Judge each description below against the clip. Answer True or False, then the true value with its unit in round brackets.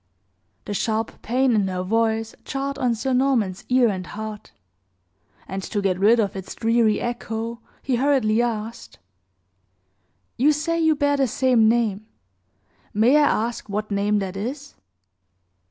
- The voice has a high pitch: True (225 Hz)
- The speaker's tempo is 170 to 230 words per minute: False (145 wpm)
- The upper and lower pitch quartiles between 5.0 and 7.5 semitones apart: False (3.6 semitones)